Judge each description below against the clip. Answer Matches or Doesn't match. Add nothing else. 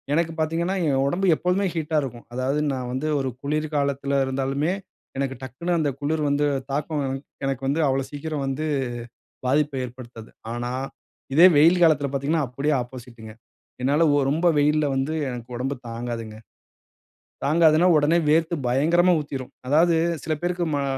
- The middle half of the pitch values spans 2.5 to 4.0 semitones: Matches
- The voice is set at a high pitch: Doesn't match